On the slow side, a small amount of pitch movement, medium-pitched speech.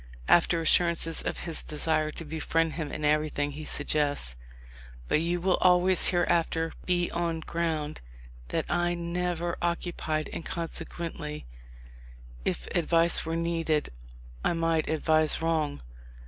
Yes: slow, 130 wpm; narrow, 1.8 semitones; medium, 165 Hz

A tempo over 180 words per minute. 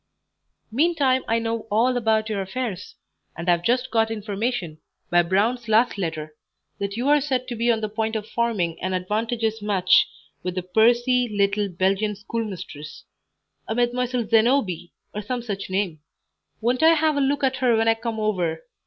No: average, 170 wpm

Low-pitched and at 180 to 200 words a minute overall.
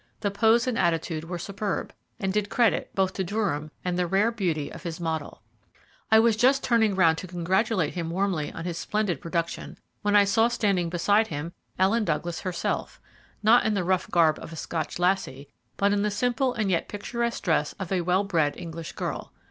No: high, 190 Hz; average, 195 wpm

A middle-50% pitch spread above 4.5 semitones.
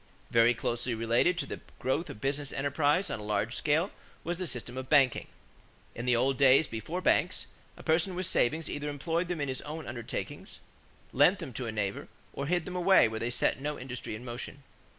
Yes: average, 5.2 semitones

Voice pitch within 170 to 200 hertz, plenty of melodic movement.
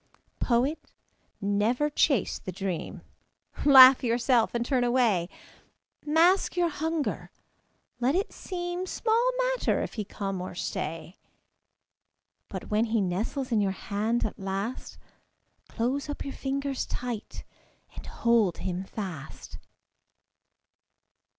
No: high, 240 Hz; wide, 5.9 semitones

